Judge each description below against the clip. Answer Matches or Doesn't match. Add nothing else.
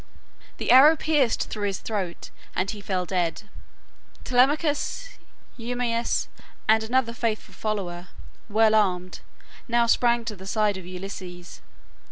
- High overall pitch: Matches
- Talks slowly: Matches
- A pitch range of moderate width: Matches